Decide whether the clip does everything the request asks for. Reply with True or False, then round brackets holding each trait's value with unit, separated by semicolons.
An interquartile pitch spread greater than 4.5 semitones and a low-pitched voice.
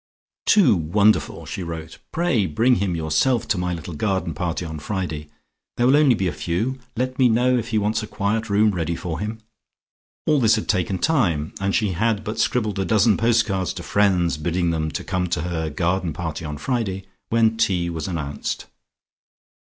True (5.0 semitones; 95 Hz)